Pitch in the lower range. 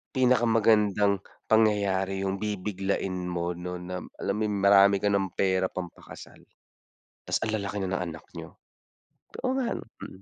Yes: low, 100 Hz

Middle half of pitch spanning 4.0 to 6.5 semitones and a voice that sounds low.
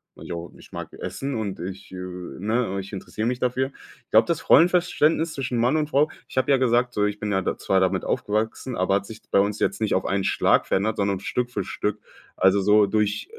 Yes: average, 4.3 semitones; low, 105 Hz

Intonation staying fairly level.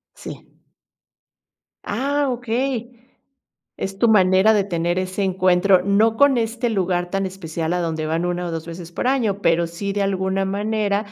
No: average, 3.8 semitones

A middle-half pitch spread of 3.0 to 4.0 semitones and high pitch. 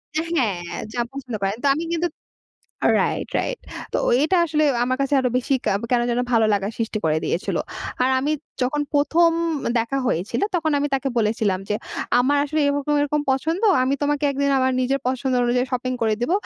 Yes: average, 3.6 semitones; very high, 265 Hz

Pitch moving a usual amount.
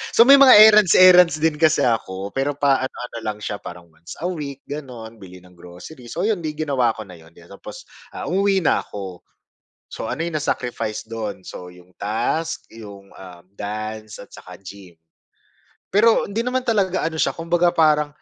No: wide, 9.0 semitones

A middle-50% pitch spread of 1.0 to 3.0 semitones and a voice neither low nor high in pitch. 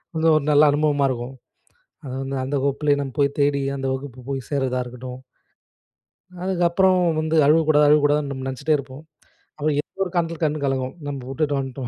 Yes: narrow, 2.4 semitones; medium, 145 Hz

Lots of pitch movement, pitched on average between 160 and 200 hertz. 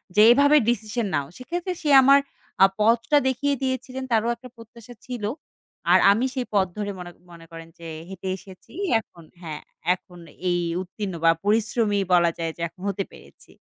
No: wide, 5.8 semitones; high, 215 Hz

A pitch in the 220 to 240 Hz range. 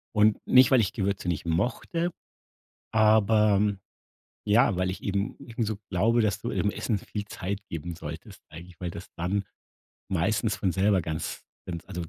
No: low, 100 Hz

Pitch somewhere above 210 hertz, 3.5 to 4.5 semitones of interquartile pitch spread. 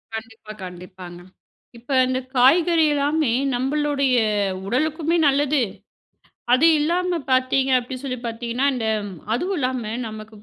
Yes: very high, 260 Hz; average, 4.2 semitones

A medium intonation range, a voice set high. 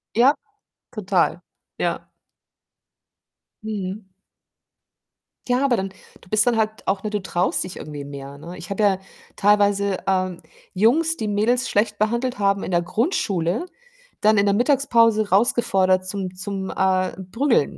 Yes: average, 3.4 semitones; high, 200 Hz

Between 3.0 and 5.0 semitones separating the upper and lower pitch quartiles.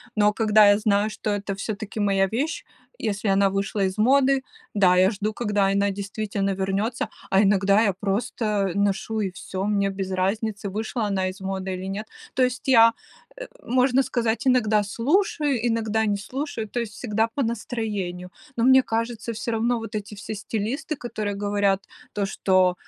No: narrow, 2.6 semitones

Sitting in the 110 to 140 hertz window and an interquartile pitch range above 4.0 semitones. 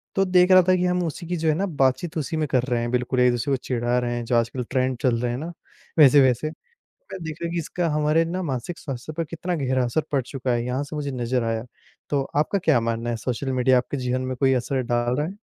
Yes: low, 135 Hz; average, 4.5 semitones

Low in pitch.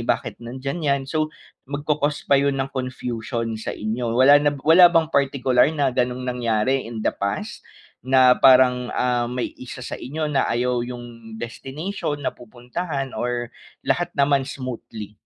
Yes: low, 130 Hz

